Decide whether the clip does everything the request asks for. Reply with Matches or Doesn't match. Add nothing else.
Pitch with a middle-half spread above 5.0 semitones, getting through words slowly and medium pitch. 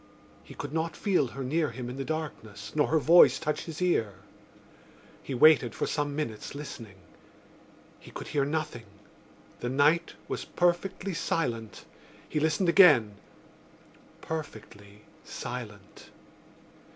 Matches